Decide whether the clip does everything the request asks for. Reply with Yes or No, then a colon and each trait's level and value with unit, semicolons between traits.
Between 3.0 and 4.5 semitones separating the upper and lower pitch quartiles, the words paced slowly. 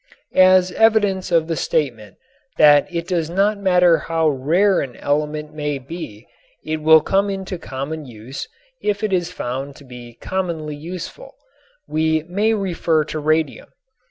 No: average, 4.0 semitones; average, 150 wpm